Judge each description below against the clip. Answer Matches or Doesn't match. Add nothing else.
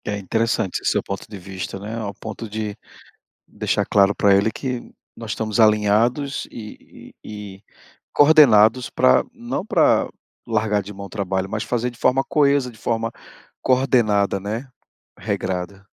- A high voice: Doesn't match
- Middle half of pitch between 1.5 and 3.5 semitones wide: Matches